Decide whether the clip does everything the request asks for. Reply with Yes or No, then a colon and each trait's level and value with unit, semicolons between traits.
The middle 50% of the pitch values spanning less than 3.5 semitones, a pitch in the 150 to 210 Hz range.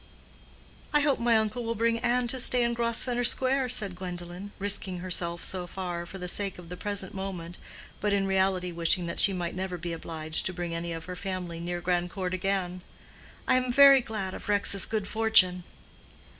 No: average, 4.0 semitones; high, 190 Hz